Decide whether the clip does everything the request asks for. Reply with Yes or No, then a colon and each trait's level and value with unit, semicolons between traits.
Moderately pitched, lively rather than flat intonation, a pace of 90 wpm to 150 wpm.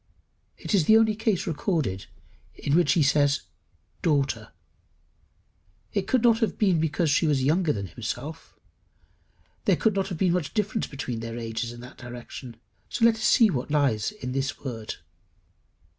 No: medium, 150 Hz; wide, 7.8 semitones; average, 160 wpm